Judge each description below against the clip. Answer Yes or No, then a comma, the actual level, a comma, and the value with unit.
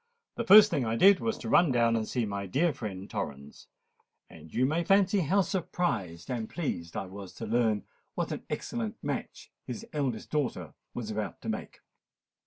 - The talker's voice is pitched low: Yes, low, 120 Hz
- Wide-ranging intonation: Yes, wide, 8.9 semitones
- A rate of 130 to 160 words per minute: No, average, 185 wpm